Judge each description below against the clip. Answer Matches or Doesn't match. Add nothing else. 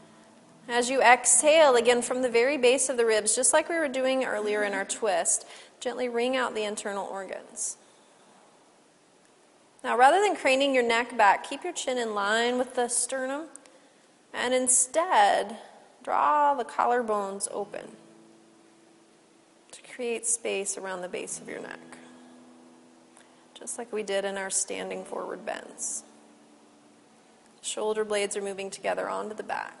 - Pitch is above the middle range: Matches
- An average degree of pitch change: Matches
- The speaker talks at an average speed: Matches